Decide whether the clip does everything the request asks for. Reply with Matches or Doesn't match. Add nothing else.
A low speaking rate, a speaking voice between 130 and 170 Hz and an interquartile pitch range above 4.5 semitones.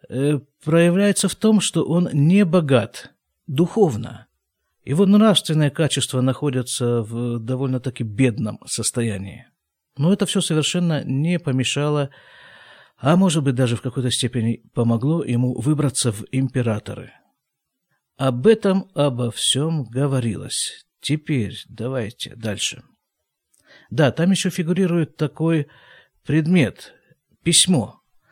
Matches